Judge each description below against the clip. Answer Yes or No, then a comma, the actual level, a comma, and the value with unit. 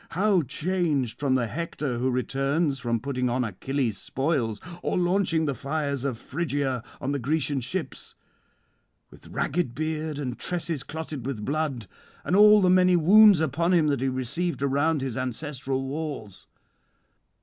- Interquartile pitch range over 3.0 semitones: Yes, average, 4.0 semitones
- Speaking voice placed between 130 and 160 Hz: Yes, medium, 140 Hz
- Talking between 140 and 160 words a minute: Yes, average, 150 wpm